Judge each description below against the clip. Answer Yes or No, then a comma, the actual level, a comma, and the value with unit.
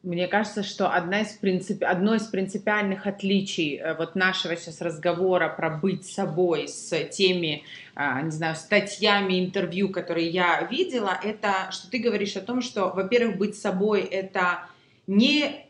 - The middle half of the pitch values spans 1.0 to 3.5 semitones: Yes, average, 2.7 semitones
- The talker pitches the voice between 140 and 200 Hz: Yes, high, 190 Hz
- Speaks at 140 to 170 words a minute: Yes, average, 145 wpm